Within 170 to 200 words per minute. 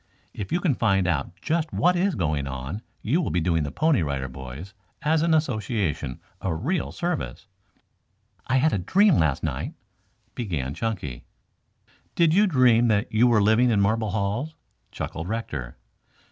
No: average, 160 wpm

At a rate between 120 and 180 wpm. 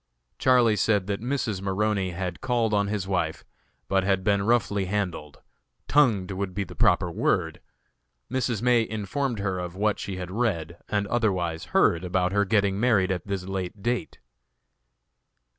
Yes: average, 160 wpm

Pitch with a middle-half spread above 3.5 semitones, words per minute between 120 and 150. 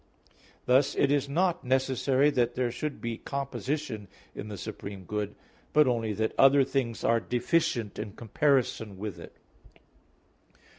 Yes: average, 4.1 semitones; average, 140 wpm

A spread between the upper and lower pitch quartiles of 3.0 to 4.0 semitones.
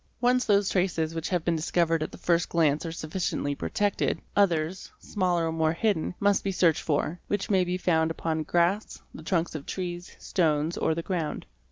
No: narrow, 2.6 semitones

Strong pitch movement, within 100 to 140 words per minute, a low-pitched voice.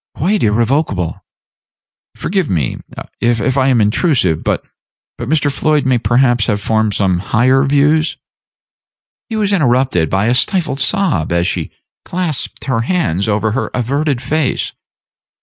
Yes: wide, 5.9 semitones; slow, 135 wpm; low, 130 Hz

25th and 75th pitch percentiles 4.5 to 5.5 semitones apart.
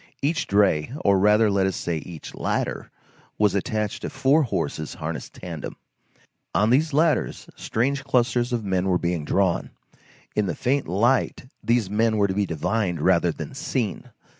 Yes: average, 5.2 semitones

